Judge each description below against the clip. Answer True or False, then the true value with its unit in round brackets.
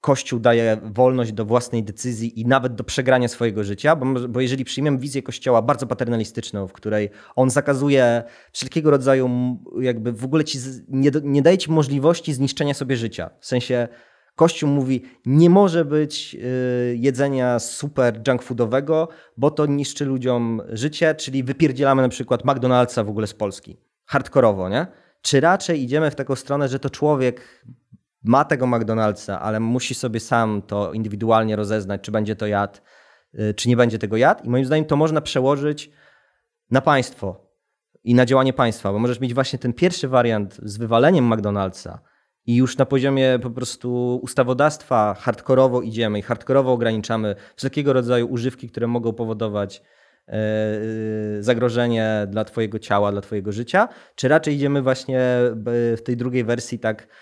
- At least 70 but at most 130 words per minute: False (155 wpm)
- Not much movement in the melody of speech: False (3.4 semitones)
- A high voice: False (125 Hz)